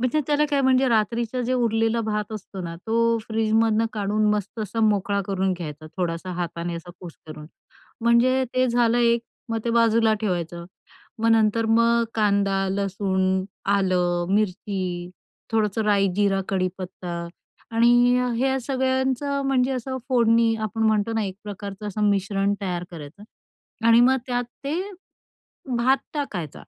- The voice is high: Yes, high, 215 Hz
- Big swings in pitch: No, average, 3.5 semitones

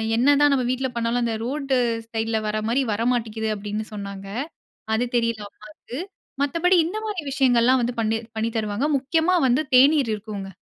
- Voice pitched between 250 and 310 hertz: No, high, 235 Hz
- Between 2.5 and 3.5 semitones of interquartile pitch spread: No, average, 3.9 semitones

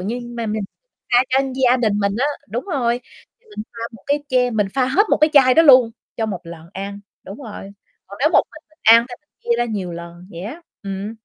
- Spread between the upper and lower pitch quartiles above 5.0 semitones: No, average, 4.4 semitones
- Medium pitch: No, high, 230 Hz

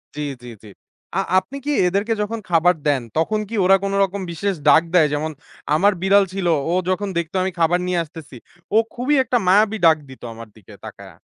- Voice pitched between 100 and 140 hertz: No, medium, 185 Hz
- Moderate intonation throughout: Yes, average, 4.2 semitones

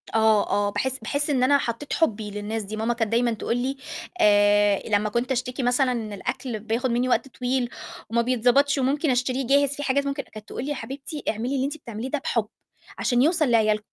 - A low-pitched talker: No, high, 245 Hz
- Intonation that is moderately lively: Yes, average, 3.7 semitones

